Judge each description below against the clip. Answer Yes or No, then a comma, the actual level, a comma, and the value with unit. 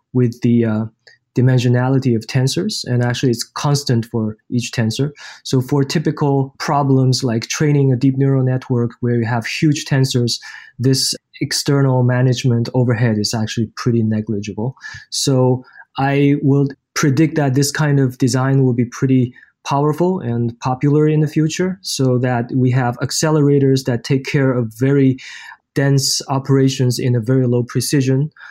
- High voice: No, low, 130 Hz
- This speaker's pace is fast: No, average, 150 wpm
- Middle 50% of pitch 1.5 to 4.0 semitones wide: Yes, narrow, 2.4 semitones